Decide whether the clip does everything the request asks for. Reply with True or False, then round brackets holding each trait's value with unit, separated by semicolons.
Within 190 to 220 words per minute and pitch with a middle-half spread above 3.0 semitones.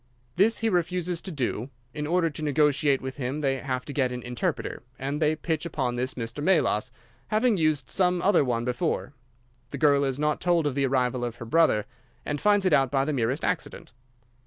True (205 wpm; 4.6 semitones)